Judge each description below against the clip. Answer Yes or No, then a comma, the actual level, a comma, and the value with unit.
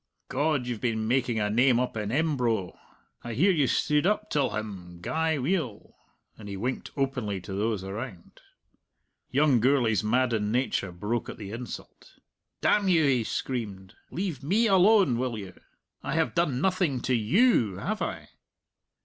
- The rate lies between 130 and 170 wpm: Yes, average, 160 wpm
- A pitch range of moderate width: No, wide, 6.0 semitones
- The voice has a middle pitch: No, low, 125 Hz